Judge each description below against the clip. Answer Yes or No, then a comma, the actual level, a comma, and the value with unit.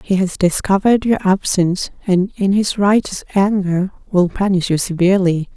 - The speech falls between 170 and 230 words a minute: No, average, 150 wpm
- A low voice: No, high, 190 Hz